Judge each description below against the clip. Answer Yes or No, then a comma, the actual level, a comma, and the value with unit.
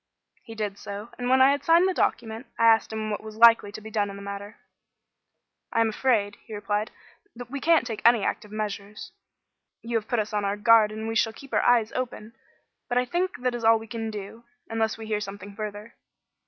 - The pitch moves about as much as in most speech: No, narrow, 2.2 semitones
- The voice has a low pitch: No, high, 220 Hz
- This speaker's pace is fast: Yes, fast, 225 wpm